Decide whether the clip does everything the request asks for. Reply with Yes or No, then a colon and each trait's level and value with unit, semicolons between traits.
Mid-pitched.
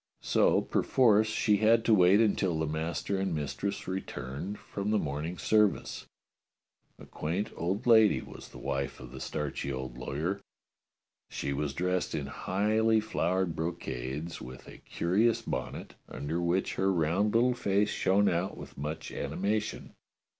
No: very low, 90 Hz